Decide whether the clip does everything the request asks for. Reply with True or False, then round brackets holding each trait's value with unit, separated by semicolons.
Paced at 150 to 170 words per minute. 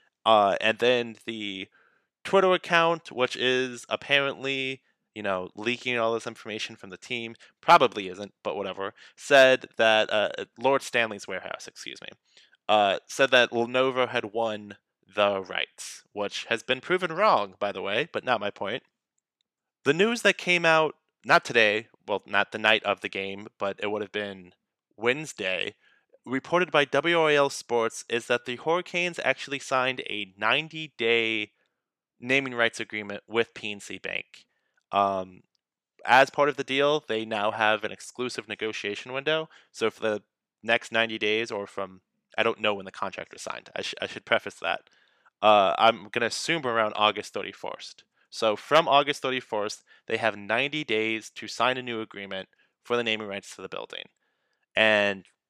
True (165 wpm)